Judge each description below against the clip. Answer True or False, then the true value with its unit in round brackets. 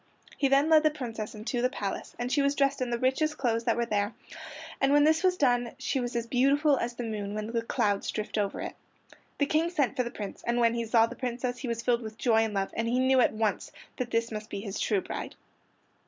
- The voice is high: True (240 Hz)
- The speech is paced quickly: True (255 wpm)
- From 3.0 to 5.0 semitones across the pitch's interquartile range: True (3.3 semitones)